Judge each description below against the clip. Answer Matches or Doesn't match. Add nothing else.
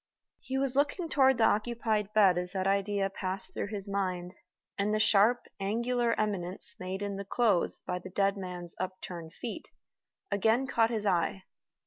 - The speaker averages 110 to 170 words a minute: Matches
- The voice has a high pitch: Matches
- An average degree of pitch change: Matches